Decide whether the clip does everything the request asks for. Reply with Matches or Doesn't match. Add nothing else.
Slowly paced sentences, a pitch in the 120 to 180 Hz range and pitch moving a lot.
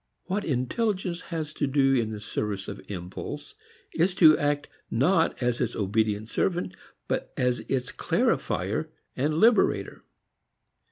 Matches